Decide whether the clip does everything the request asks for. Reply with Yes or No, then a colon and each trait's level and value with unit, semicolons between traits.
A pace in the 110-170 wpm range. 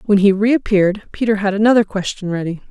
No: average, 180 wpm